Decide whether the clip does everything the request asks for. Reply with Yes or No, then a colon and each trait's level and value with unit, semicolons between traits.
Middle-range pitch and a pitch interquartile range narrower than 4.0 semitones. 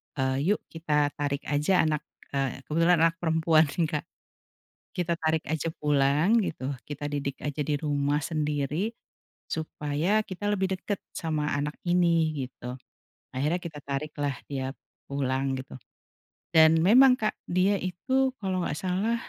Yes: medium, 155 Hz; average, 3.6 semitones